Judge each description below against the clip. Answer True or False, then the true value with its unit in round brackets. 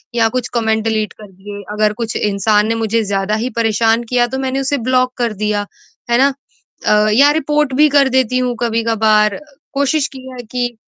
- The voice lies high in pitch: True (230 Hz)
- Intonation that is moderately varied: True (3.3 semitones)